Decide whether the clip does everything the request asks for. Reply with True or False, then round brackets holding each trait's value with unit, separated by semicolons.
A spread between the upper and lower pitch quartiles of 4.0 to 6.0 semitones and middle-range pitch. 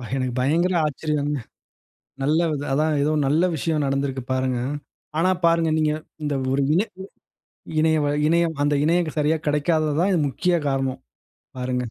False (2.9 semitones; 150 Hz)